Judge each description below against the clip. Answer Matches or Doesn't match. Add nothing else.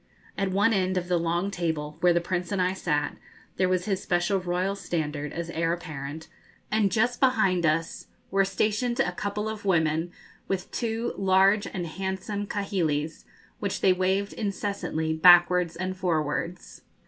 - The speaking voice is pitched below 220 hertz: Matches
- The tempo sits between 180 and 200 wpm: Doesn't match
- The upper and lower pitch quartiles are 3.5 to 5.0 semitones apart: Doesn't match